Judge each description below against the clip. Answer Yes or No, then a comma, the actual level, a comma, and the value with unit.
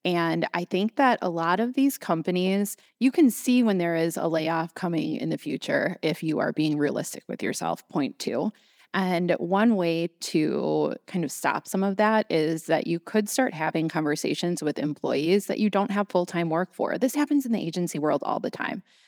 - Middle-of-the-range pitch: Yes, medium, 180 Hz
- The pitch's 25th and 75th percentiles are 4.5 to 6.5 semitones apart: Yes, average, 4.9 semitones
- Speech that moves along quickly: Yes, fast, 210 wpm